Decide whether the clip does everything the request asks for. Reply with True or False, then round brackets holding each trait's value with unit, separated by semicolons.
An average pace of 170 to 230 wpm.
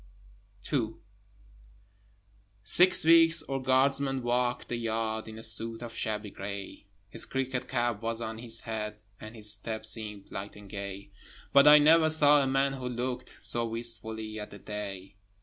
False (160 wpm)